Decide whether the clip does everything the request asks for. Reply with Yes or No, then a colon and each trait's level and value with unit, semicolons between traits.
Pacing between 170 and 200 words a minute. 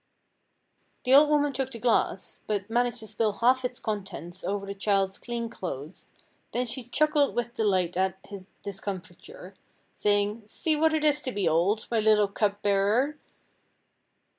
No: average, 160 wpm